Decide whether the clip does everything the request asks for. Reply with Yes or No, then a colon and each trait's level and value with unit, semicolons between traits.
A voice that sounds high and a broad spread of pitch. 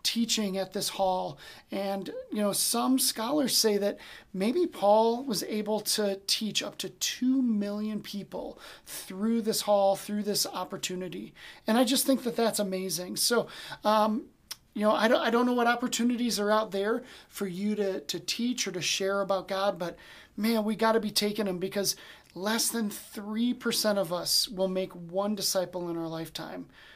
No: high, 210 Hz; average, 3.1 semitones